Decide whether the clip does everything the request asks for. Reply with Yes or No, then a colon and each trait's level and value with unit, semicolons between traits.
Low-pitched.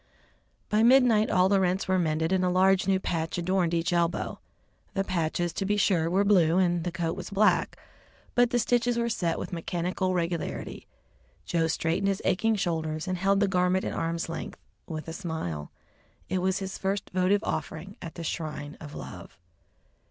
No: medium, 180 Hz